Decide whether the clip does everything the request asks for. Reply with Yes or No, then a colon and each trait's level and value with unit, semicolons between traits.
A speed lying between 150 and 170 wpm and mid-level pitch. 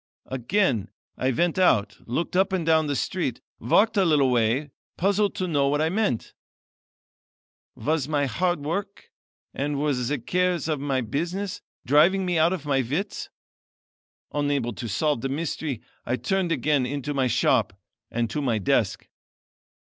Yes: average, 155 wpm; medium, 150 Hz